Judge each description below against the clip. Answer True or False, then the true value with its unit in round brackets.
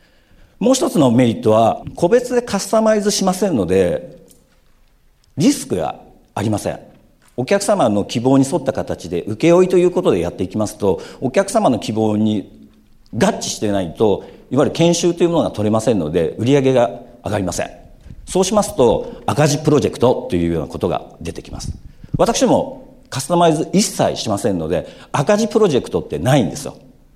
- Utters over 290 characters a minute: True (370 characters per minute)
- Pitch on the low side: False (155 Hz)